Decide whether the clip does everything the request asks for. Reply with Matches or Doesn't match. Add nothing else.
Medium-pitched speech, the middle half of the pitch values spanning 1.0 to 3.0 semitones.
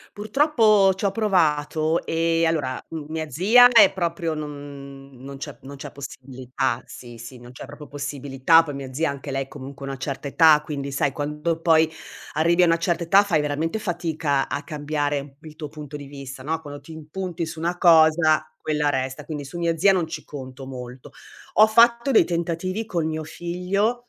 Doesn't match